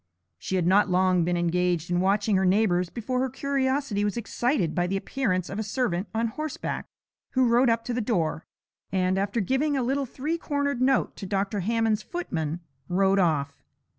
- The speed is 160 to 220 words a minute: Yes, average, 185 wpm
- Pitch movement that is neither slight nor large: No, wide, 5.9 semitones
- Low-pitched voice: No, high, 205 Hz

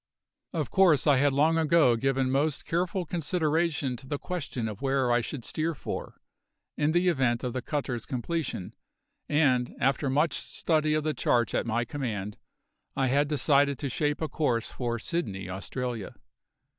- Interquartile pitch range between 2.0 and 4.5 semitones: Yes, average, 4.1 semitones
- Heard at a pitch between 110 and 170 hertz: Yes, medium, 140 Hz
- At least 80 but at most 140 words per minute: No, average, 165 wpm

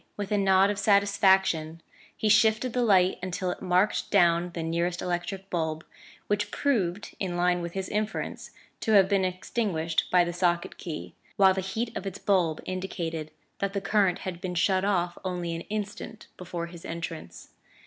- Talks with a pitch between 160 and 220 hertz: Yes, medium, 185 Hz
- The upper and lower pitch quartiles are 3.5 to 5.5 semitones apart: No, narrow, 2.6 semitones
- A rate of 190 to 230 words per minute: No, average, 175 wpm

